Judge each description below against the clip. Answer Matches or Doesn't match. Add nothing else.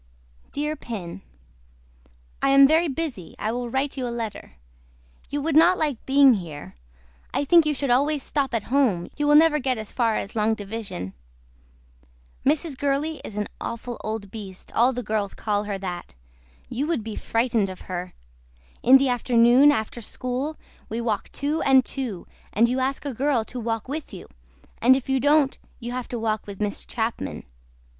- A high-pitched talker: Matches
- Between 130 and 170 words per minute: Doesn't match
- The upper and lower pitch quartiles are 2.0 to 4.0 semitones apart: Doesn't match